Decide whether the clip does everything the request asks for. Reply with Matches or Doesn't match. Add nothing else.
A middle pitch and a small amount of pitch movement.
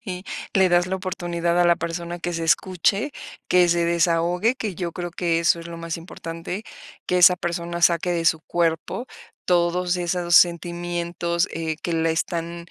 Matches